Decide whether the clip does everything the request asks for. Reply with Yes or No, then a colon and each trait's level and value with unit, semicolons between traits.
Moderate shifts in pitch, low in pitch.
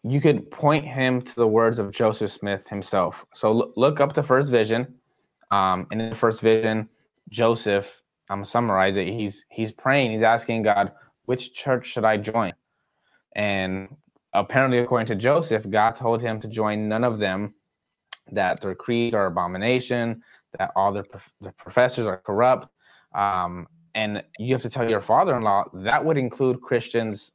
Yes: average, 3.5 semitones; low, 110 Hz